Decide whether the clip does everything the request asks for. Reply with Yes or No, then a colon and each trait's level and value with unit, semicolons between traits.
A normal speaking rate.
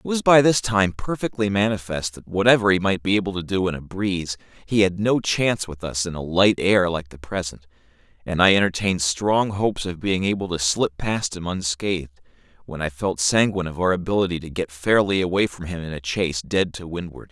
No: fast, 220 wpm